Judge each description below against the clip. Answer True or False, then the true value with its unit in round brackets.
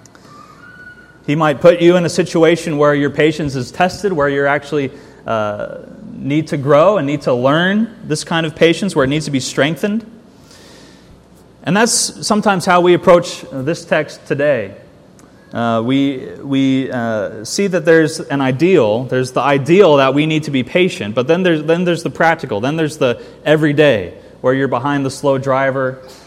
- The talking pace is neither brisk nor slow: True (175 wpm)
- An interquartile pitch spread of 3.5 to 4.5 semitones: True (4.2 semitones)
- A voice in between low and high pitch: True (155 Hz)